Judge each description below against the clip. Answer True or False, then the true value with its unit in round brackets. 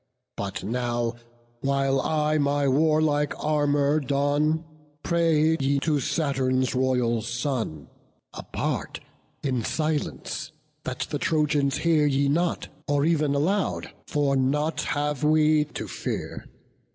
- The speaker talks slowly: True (115 wpm)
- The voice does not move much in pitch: True (2.3 semitones)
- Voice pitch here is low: False (145 Hz)